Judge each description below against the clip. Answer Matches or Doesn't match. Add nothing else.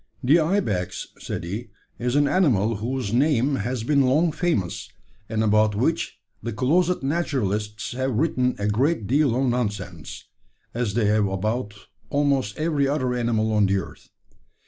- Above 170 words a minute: Doesn't match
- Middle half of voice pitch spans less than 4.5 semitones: Doesn't match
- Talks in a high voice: Doesn't match